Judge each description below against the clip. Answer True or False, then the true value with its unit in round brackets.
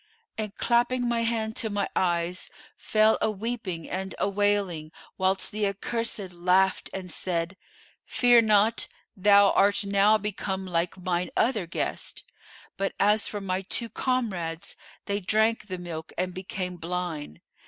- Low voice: False (195 Hz)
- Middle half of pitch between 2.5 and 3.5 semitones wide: True (3.1 semitones)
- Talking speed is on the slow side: False (145 wpm)